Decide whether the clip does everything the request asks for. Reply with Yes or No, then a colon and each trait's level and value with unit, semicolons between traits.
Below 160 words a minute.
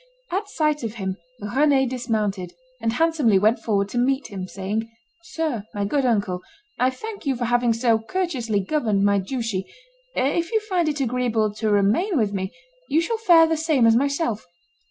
No: average, 175 wpm